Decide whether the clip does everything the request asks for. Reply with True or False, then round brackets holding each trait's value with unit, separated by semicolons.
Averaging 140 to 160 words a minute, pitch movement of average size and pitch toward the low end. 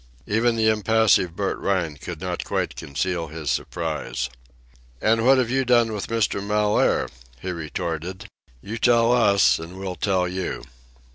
True (150 wpm; 4.5 semitones; 100 Hz)